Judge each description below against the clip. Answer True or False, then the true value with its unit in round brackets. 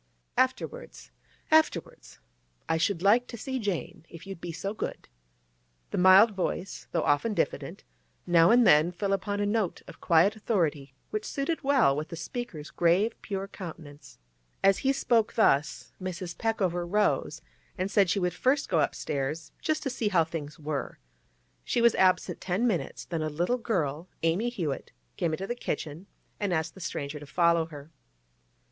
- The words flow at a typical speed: True (160 wpm)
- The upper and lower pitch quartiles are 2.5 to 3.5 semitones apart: False (5.0 semitones)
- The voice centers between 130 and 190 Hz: True (185 Hz)